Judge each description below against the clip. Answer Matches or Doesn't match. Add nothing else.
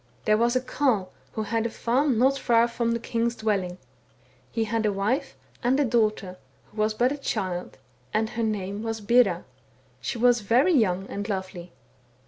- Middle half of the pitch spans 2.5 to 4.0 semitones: Matches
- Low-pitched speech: Doesn't match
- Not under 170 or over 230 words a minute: Matches